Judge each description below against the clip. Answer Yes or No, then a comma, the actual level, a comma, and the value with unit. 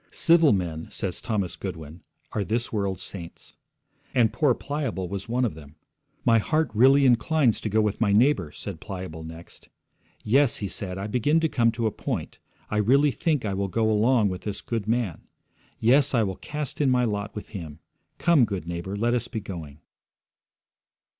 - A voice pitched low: Yes, low, 110 Hz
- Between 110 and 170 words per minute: No, average, 185 wpm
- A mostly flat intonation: No, average, 4.7 semitones